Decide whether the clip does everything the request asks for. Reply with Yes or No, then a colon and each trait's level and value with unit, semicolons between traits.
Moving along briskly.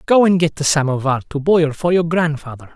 Yes: fast, 220 wpm